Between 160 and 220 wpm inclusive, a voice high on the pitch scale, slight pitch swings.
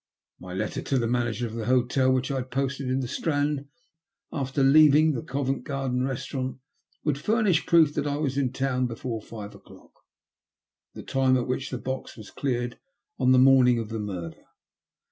No: average, 190 wpm; low, 130 Hz; narrow, 2.3 semitones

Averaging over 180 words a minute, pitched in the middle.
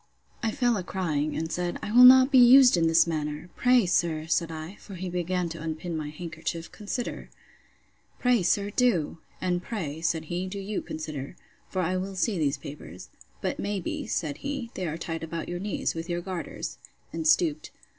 Yes: average, 190 wpm; medium, 175 Hz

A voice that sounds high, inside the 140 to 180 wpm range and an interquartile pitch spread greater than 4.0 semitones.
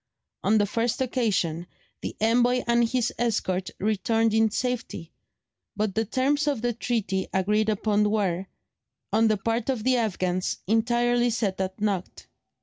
No: high, 220 Hz; average, 145 wpm; average, 3.4 semitones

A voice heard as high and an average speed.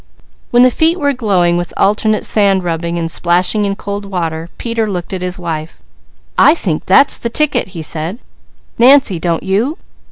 Yes: high, 195 Hz; average, 170 wpm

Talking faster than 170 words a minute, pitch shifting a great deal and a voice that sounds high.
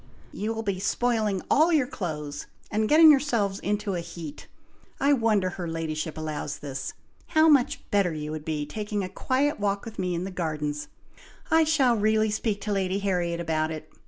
Yes: average, 185 wpm; wide, 5.8 semitones; high, 200 Hz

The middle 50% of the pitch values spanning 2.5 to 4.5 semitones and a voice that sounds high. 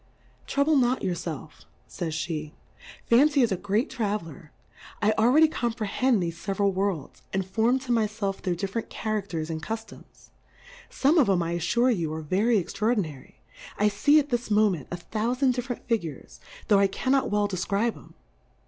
No: average, 5.3 semitones; high, 210 Hz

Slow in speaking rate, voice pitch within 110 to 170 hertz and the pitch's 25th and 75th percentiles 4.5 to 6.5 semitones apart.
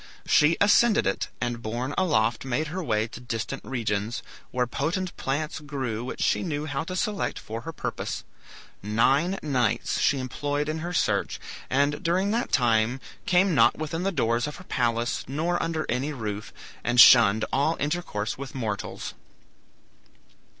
No: average, 155 wpm; low, 135 Hz; wide, 5.5 semitones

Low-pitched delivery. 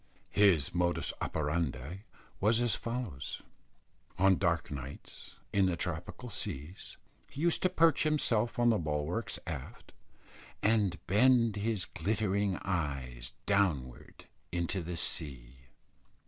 Yes: very low, 90 Hz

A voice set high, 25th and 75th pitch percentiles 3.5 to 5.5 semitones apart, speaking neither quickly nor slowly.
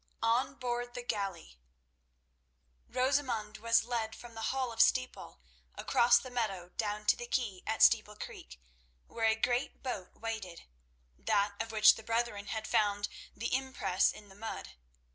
No: high, 225 Hz; average, 3.0 semitones; average, 150 wpm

